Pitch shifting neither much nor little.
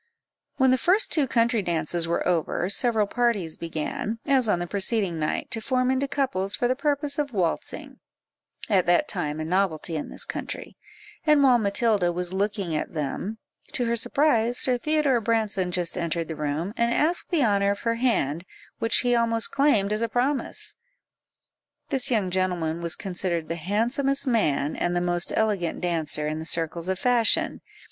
No: wide, 6.0 semitones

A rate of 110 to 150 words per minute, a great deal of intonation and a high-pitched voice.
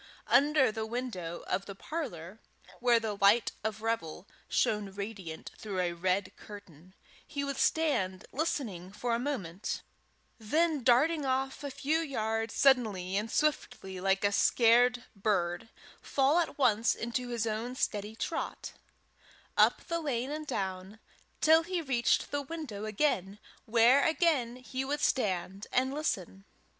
Yes: average, 140 wpm; wide, 5.7 semitones; high, 230 Hz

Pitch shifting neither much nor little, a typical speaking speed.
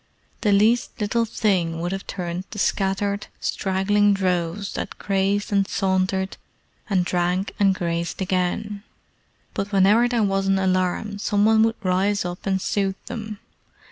No: narrow, 1.9 semitones; average, 145 wpm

